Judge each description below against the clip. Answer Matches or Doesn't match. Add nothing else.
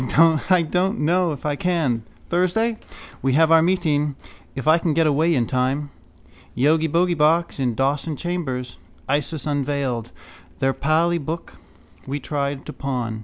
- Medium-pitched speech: Matches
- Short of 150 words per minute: Matches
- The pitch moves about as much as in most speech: Matches